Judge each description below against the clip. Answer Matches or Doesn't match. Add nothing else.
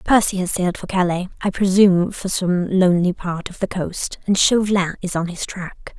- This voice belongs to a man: Doesn't match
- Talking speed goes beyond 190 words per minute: Matches